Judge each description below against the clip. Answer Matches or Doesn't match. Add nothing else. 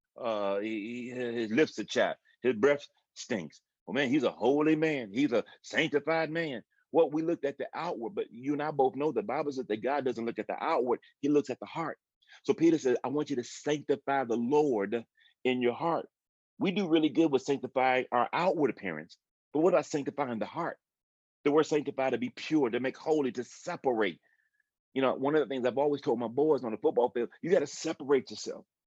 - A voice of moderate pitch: Matches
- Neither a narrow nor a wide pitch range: Matches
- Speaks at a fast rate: Matches